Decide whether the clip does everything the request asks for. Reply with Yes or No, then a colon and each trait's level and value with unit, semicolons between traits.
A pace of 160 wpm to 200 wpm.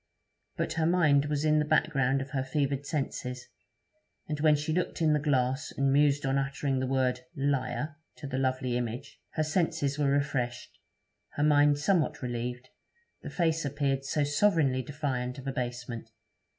Yes: average, 165 wpm